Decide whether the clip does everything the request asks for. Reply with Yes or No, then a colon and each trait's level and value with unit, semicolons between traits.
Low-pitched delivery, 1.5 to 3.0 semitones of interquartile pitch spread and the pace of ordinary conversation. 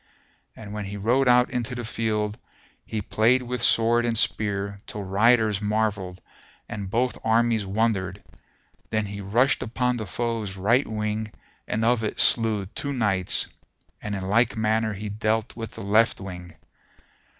Yes: low, 110 Hz; narrow, 2.4 semitones; average, 155 wpm